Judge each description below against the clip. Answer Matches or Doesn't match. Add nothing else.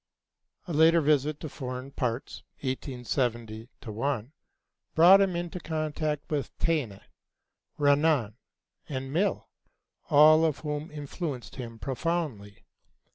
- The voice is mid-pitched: Matches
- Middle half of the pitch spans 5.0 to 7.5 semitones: Doesn't match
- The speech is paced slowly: Matches